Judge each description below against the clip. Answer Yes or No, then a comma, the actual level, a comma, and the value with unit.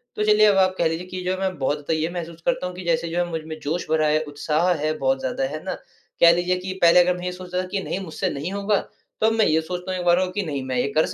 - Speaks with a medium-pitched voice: Yes, medium, 175 Hz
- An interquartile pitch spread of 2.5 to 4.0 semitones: Yes, average, 2.9 semitones